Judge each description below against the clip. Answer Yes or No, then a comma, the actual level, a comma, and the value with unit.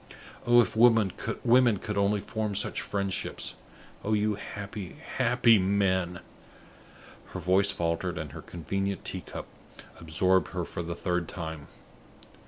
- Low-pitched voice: Yes, low, 100 Hz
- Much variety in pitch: No, average, 3.1 semitones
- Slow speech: Yes, slow, 130 wpm